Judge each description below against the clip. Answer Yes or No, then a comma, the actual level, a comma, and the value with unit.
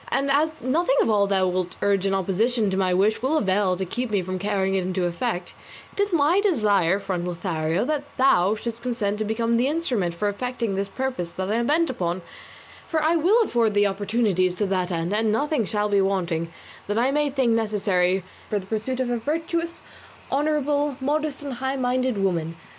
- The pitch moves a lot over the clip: Yes, wide, 5.8 semitones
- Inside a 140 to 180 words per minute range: No, fast, 205 wpm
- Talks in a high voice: Yes, high, 215 Hz